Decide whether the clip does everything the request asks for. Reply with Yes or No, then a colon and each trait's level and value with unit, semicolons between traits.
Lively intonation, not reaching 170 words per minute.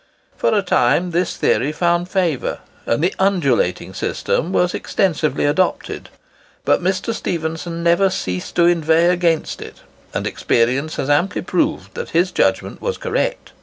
No: average, 3.4 semitones; average, 145 wpm